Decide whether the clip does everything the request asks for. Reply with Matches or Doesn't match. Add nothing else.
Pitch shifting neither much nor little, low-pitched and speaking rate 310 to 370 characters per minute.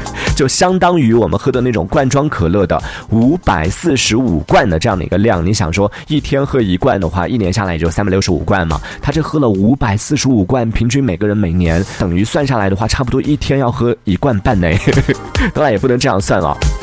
Doesn't match